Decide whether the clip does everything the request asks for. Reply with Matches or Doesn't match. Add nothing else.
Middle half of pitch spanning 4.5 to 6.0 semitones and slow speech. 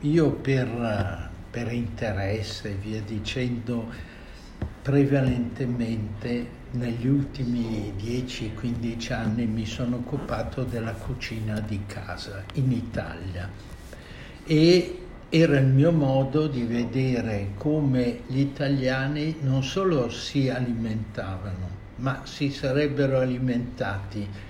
Doesn't match